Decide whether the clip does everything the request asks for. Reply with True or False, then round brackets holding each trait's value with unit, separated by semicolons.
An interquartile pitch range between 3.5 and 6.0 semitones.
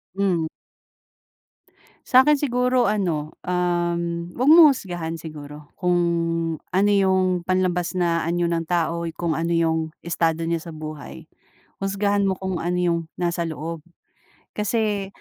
False (2.8 semitones)